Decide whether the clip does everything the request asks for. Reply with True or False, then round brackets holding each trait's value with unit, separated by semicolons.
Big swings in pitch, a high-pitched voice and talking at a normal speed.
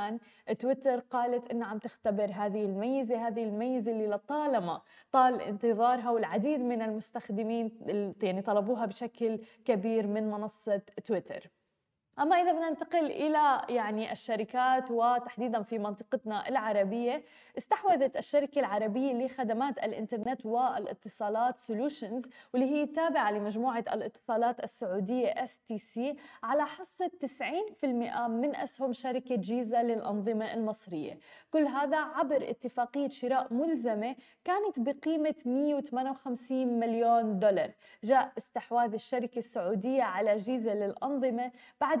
False (3.4 semitones; 245 Hz; 110 wpm)